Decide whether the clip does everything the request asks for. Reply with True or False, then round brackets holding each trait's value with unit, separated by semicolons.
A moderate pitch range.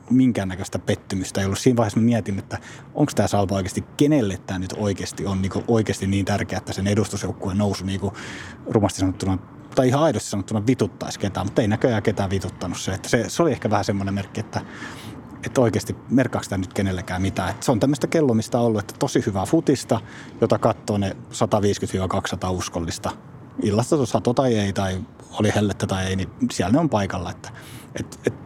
True (3.4 semitones)